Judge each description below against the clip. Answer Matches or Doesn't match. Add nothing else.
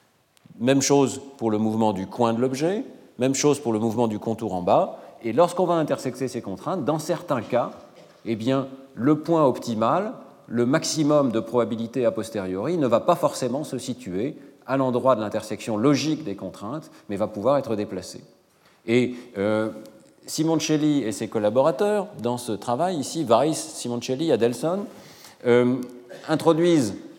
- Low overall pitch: Matches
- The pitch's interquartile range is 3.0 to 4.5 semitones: Doesn't match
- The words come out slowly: Doesn't match